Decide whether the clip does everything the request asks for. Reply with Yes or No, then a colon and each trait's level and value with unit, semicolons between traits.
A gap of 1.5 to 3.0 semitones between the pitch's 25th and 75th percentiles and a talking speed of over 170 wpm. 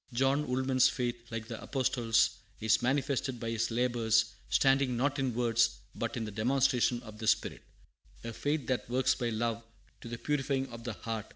Yes: narrow, 2.6 semitones; average, 180 wpm